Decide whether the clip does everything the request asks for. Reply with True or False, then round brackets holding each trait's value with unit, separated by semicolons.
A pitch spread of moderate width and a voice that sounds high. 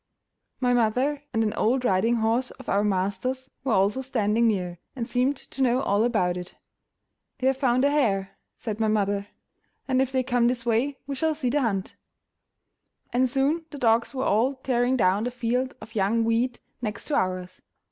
True (3.7 semitones; 240 Hz)